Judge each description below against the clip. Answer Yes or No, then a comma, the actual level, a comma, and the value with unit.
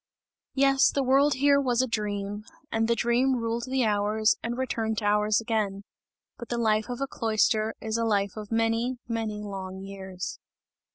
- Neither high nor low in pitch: No, high, 225 Hz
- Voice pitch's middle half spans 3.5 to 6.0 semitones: No, average, 2.7 semitones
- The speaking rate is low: No, average, 175 wpm